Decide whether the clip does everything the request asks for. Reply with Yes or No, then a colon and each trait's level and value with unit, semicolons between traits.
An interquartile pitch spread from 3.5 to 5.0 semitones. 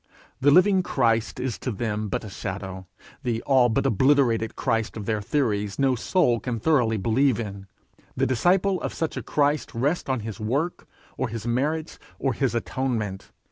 Yes: average, 4.4 semitones